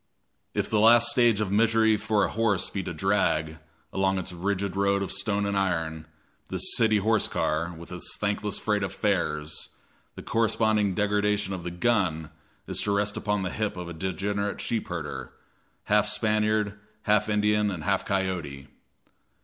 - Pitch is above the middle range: No, low, 100 Hz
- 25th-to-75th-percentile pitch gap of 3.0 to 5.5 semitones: No, narrow, 2.5 semitones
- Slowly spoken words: No, average, 165 wpm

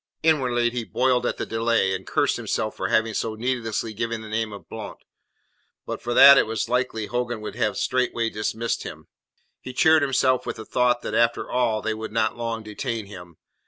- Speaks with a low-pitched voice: Yes, low, 115 Hz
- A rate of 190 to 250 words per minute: Yes, average, 195 wpm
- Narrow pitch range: Yes, narrow, 2.2 semitones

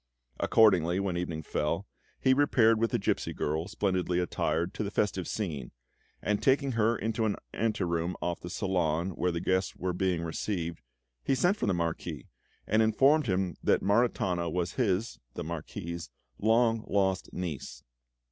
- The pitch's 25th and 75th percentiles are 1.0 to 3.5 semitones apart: No, average, 4.4 semitones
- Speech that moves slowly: No, average, 160 wpm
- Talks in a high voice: No, very low, 95 Hz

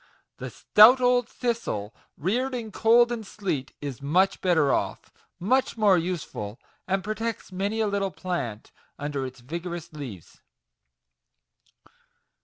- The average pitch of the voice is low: No, medium, 185 Hz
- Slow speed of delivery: Yes, slow, 125 wpm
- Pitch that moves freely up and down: Yes, wide, 7.4 semitones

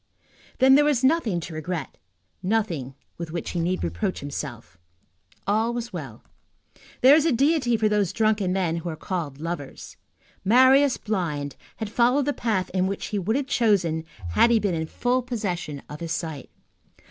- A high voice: Yes, high, 195 Hz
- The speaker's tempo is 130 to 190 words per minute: Yes, average, 170 wpm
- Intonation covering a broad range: Yes, wide, 6.5 semitones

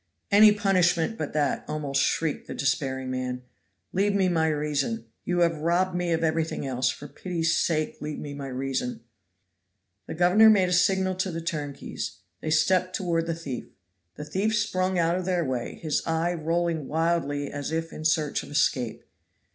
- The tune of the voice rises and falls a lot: No, average, 3.8 semitones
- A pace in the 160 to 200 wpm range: Yes, average, 175 wpm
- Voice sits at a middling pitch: Yes, medium, 165 Hz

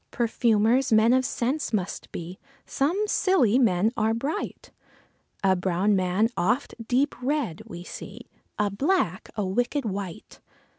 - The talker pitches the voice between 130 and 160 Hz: No, high, 225 Hz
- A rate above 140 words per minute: No, slow, 135 wpm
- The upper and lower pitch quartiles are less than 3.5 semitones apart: No, wide, 5.5 semitones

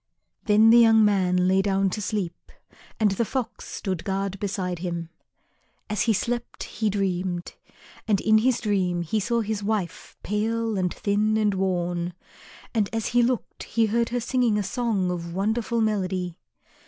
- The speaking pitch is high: Yes, high, 205 Hz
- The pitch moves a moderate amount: Yes, average, 3.2 semitones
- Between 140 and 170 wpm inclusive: Yes, average, 165 wpm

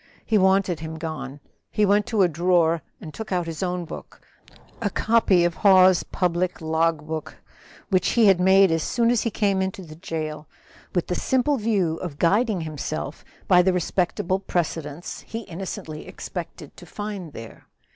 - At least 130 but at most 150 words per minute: No, average, 170 wpm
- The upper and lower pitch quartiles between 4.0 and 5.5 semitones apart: No, average, 3.5 semitones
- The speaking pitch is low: No, medium, 180 Hz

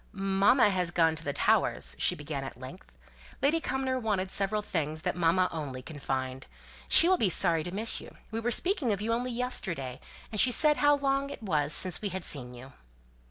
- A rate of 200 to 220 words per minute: Yes, fast, 205 wpm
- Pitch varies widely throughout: Yes, wide, 7.7 semitones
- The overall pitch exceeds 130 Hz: Yes, high, 190 Hz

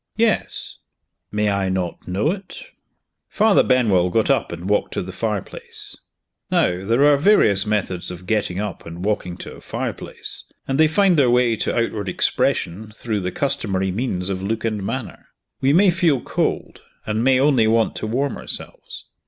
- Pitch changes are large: Yes, wide, 5.8 semitones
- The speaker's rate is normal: Yes, average, 170 wpm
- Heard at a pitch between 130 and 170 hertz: No, low, 110 Hz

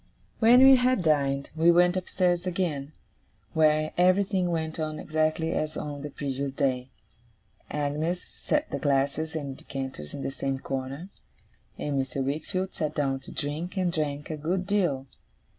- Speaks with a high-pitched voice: No, medium, 155 Hz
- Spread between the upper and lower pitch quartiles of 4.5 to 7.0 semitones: No, average, 4.1 semitones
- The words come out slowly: No, average, 155 wpm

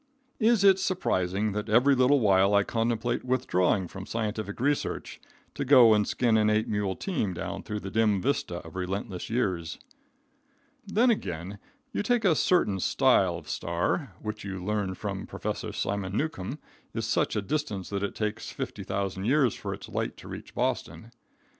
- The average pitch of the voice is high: No, low, 105 Hz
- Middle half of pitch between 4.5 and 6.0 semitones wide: Yes, average, 5.0 semitones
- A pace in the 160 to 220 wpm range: Yes, average, 165 wpm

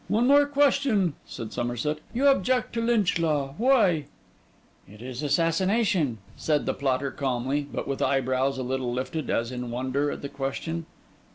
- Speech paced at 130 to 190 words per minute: Yes, average, 160 wpm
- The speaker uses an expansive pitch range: Yes, wide, 7.4 semitones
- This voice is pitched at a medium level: Yes, medium, 145 Hz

